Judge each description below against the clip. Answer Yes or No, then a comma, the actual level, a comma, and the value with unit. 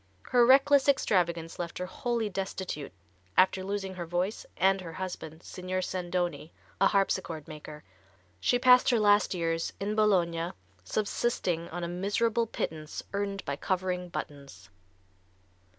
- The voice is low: No, medium, 185 Hz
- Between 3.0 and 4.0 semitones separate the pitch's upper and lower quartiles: Yes, average, 3.4 semitones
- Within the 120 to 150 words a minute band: Yes, slow, 135 wpm